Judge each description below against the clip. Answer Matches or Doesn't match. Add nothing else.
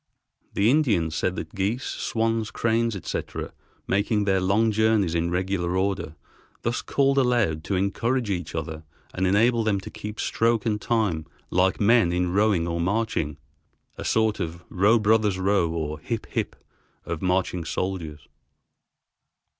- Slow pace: Doesn't match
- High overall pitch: Doesn't match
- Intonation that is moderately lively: Matches